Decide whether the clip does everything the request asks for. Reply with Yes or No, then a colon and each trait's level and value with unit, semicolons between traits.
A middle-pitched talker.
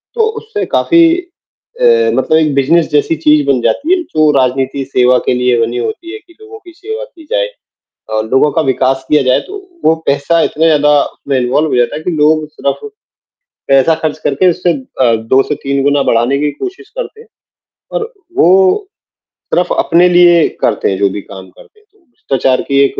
Yes: medium, 150 Hz